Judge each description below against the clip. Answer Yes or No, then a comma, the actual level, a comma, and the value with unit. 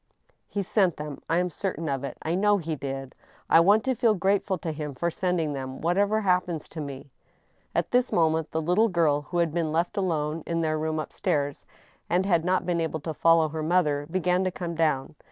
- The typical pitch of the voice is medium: Yes, medium, 165 Hz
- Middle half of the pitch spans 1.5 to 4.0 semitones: Yes, average, 3.1 semitones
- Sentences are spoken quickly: Yes, fast, 225 wpm